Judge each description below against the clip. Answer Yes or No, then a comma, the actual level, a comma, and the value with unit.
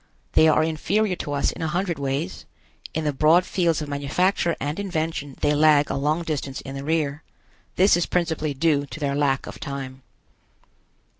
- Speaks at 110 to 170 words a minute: No, average, 180 wpm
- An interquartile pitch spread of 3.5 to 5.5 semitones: No, average, 2.8 semitones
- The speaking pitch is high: No, medium, 155 Hz